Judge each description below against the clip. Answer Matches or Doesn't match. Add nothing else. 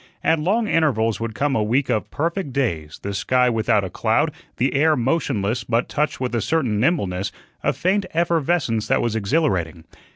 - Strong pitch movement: Matches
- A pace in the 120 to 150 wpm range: Doesn't match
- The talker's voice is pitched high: Doesn't match